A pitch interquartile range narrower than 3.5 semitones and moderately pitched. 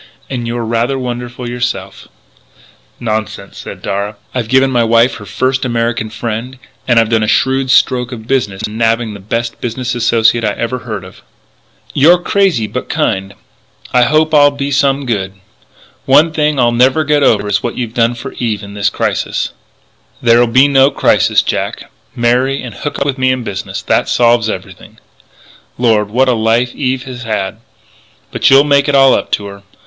No: average, 2.9 semitones; low, 120 Hz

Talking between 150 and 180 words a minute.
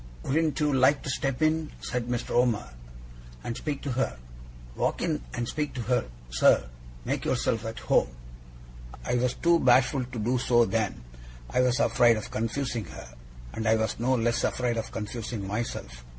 Yes: average, 175 wpm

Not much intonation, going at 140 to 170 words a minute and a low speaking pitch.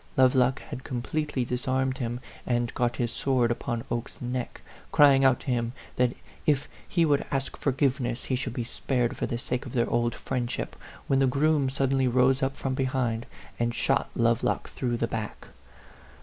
No: narrow, 2.0 semitones; average, 185 wpm; low, 125 Hz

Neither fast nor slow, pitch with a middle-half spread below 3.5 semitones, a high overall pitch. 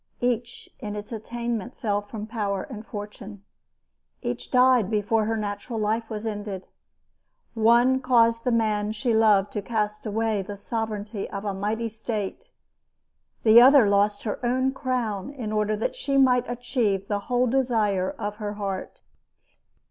Yes: average, 150 wpm; narrow, 2.6 semitones; high, 220 Hz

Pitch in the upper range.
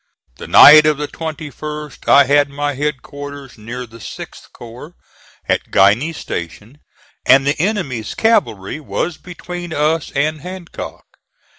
No: medium, 145 Hz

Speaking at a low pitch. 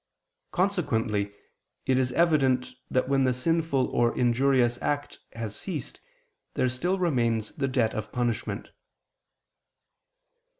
Yes: low, 130 Hz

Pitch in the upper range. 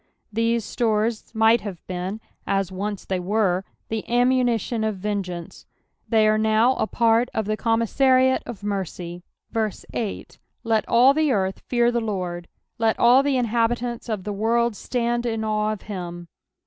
Yes: high, 220 Hz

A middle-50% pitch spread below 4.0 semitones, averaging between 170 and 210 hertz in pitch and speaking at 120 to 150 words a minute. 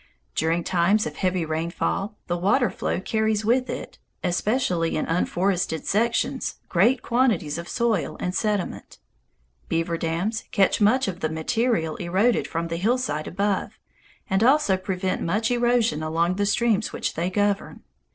No: average, 4.6 semitones; high, 190 Hz; average, 145 wpm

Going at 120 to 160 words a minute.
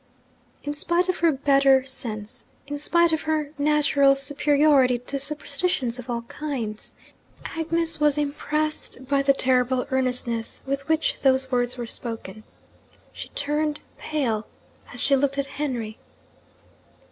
Yes: slow, 135 wpm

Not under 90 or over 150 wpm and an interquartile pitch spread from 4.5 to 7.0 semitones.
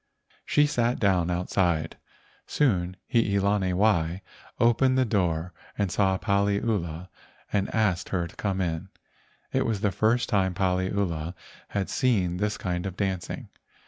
No: average, 140 wpm; average, 2.9 semitones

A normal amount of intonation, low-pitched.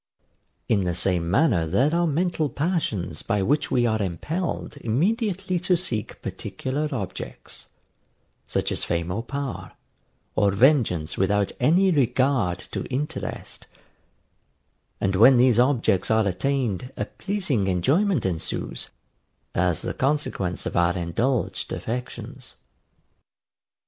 No: wide, 7.8 semitones; low, 120 Hz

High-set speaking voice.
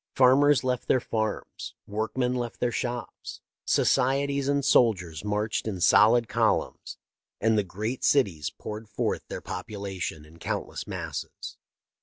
No: low, 110 Hz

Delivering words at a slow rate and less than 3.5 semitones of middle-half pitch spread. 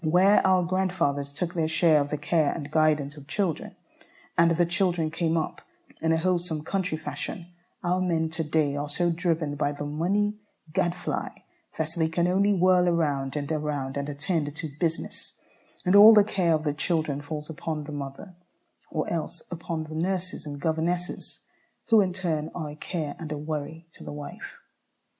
No: average, 180 wpm; average, 3.0 semitones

